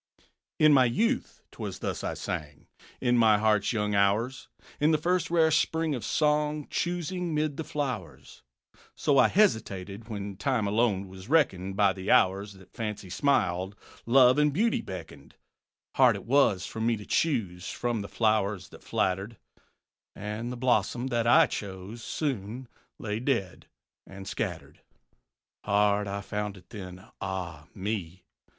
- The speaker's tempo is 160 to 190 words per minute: No, average, 150 wpm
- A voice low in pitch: Yes, low, 110 Hz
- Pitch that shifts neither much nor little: No, wide, 5.8 semitones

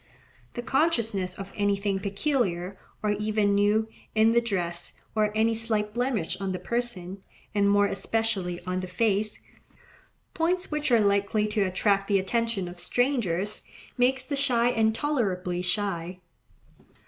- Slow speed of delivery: Yes, slow, 130 wpm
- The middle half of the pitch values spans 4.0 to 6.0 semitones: No, average, 3.3 semitones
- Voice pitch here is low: No, high, 210 Hz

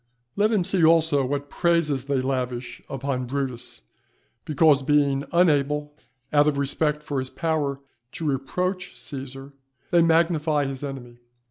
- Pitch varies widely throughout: No, average, 3.0 semitones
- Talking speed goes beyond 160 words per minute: No, slow, 135 wpm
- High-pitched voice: No, medium, 145 Hz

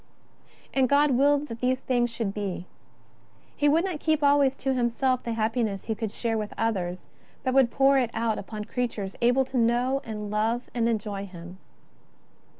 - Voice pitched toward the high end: Yes, high, 235 Hz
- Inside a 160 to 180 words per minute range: Yes, average, 170 wpm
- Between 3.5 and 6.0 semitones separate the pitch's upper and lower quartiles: Yes, average, 3.8 semitones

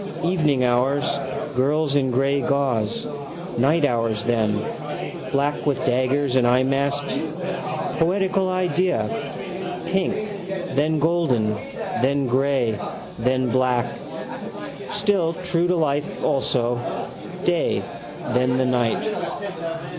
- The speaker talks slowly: Yes, slow, 95 wpm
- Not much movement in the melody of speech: No, average, 4.8 semitones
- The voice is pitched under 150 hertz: Yes, medium, 140 Hz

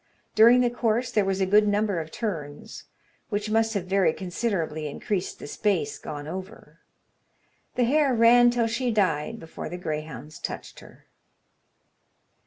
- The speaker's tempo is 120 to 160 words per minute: Yes, average, 150 wpm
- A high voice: Yes, high, 205 Hz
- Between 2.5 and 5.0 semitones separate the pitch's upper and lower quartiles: No, wide, 5.6 semitones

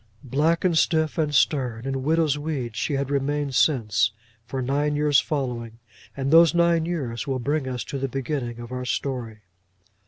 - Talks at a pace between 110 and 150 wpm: No, average, 175 wpm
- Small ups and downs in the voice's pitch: No, average, 3.3 semitones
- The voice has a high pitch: No, medium, 140 Hz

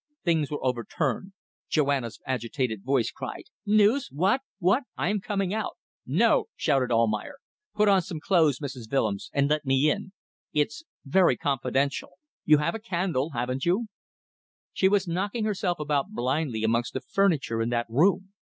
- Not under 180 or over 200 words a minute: No, average, 155 wpm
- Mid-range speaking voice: Yes, medium, 150 Hz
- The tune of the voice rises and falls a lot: Yes, wide, 6.9 semitones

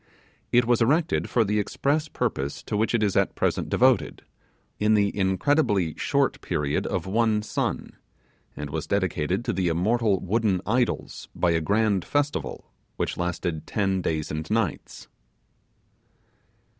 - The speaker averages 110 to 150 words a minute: Yes, average, 145 wpm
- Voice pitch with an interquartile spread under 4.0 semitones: No, average, 4.7 semitones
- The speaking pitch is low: Yes, low, 100 Hz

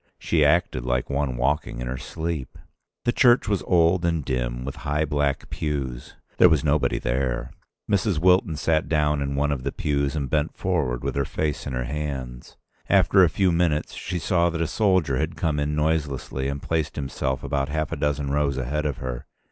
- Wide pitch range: No, average, 3.3 semitones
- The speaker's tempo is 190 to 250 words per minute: Yes, average, 195 wpm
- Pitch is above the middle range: No, very low, 75 Hz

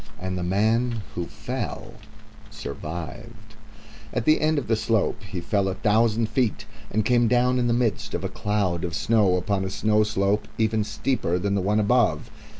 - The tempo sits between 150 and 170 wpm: No, average, 180 wpm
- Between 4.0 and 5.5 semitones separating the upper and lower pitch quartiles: No, average, 3.1 semitones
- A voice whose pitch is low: Yes, low, 105 Hz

